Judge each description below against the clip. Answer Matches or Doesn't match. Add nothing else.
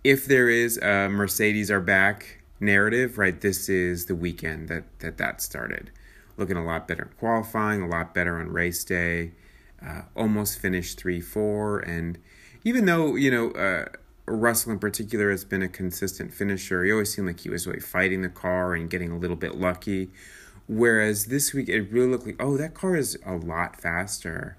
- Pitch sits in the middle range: Doesn't match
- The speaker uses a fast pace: Doesn't match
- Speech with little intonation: Doesn't match